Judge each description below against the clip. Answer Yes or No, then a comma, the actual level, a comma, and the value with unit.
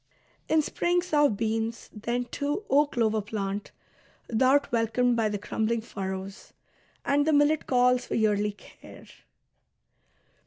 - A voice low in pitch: No, high, 235 Hz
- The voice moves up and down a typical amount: Yes, average, 5.0 semitones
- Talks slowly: Yes, slow, 125 wpm